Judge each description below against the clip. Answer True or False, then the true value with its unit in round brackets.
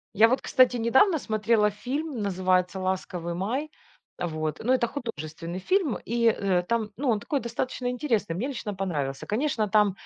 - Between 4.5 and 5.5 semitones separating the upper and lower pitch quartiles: True (5.2 semitones)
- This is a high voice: True (215 Hz)